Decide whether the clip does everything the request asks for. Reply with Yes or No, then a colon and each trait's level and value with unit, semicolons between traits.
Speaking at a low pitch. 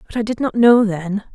No: high, 215 Hz